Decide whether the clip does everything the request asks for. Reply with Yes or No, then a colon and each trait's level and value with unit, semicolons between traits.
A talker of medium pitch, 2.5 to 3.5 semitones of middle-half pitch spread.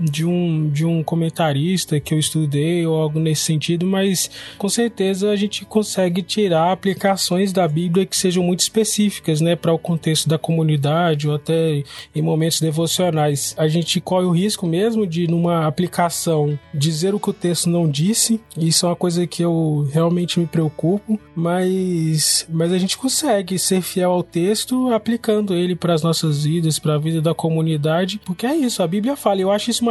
Yes: medium, 170 Hz; average, 3.1 semitones